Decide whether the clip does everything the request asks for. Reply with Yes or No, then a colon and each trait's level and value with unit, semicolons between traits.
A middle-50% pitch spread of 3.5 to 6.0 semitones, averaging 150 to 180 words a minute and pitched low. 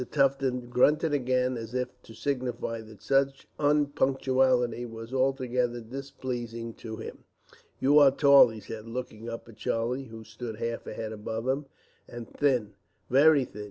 No: average, 3.0 semitones; average, 155 wpm; low, 125 Hz